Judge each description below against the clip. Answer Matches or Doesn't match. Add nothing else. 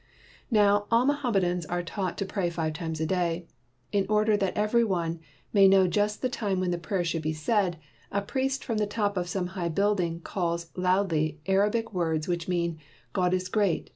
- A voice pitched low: Doesn't match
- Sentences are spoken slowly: Doesn't match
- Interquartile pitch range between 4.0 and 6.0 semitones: Doesn't match